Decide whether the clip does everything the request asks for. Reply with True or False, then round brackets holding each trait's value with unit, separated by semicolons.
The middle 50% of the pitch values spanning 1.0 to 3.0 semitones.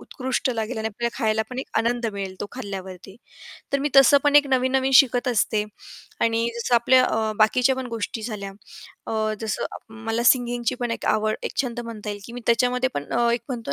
True (2.7 semitones)